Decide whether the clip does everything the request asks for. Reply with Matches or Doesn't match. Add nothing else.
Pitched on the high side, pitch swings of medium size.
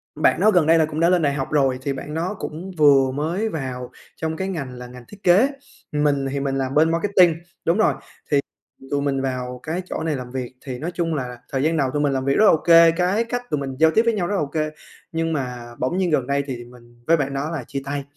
Doesn't match